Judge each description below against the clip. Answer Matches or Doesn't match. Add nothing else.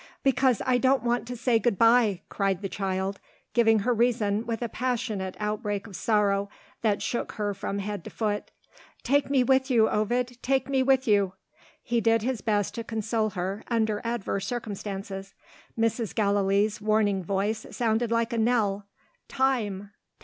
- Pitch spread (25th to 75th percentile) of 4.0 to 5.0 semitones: Doesn't match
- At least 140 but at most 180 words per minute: Matches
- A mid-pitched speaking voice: Doesn't match